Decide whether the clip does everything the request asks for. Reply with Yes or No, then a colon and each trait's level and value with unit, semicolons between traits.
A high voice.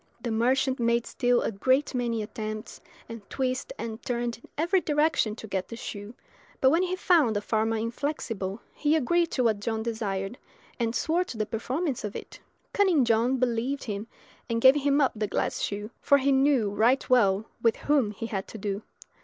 Yes: high, 235 Hz